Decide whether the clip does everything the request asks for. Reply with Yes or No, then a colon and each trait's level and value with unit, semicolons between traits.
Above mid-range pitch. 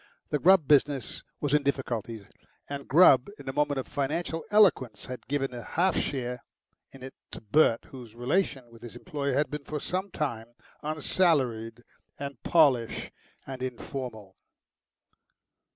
No: low, 135 Hz